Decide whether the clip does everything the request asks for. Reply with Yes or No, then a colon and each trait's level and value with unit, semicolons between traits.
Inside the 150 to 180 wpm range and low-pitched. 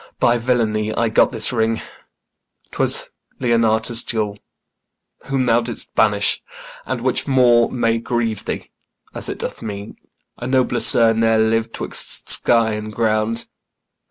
No: slow, 135 wpm; low, 115 Hz